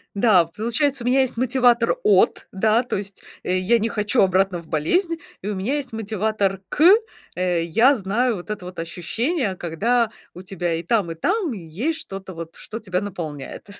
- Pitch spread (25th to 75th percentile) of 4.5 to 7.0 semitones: Yes, average, 5.0 semitones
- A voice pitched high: Yes, high, 205 Hz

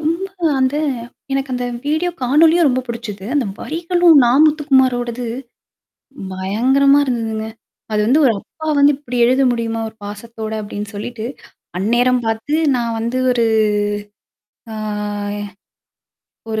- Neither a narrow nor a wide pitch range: Yes, average, 4.1 semitones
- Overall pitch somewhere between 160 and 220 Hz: No, high, 245 Hz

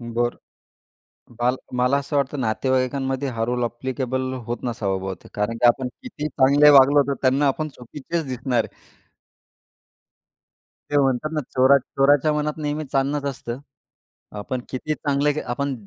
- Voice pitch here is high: No, low, 130 Hz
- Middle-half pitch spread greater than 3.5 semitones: No, average, 2.7 semitones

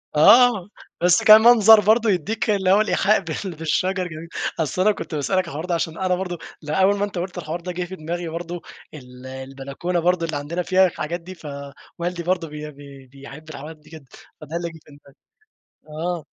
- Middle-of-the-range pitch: Yes, medium, 170 Hz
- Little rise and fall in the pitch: No, average, 3.5 semitones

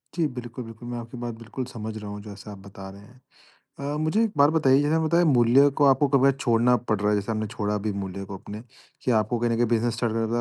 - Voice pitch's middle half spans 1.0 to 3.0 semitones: No, average, 4.0 semitones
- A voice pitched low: Yes, low, 120 Hz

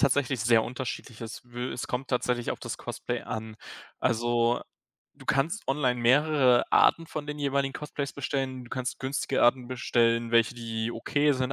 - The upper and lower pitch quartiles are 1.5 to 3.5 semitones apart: Yes, average, 2.7 semitones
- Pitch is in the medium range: No, low, 125 Hz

